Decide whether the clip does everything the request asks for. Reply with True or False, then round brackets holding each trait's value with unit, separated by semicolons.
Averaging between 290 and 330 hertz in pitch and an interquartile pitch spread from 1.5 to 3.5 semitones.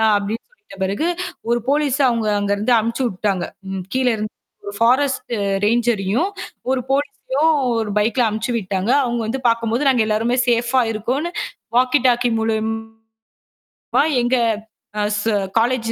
False (230 Hz; 3.0 semitones)